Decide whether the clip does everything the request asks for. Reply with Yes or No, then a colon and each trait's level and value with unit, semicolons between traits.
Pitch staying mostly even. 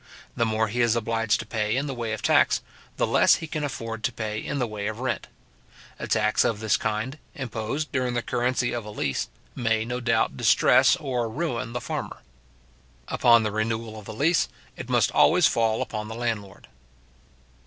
Yes: narrow, 2.2 semitones